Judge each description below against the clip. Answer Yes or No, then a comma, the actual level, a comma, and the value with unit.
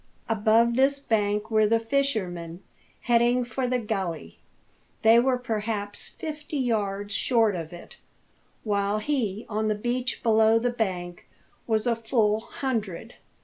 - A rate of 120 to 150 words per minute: Yes, slow, 135 wpm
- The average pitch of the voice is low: No, high, 220 Hz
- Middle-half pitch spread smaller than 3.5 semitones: Yes, average, 3.0 semitones